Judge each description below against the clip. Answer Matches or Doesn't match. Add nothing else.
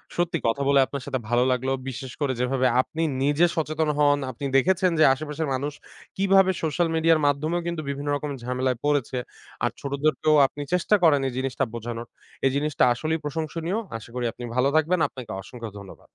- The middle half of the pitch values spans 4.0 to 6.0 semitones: Doesn't match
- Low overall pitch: Doesn't match